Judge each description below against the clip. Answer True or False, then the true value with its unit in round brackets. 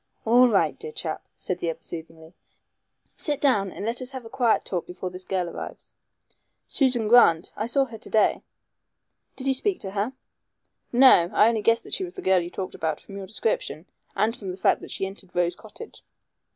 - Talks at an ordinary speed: False (210 wpm)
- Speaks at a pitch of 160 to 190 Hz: False (215 Hz)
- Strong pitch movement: True (5.7 semitones)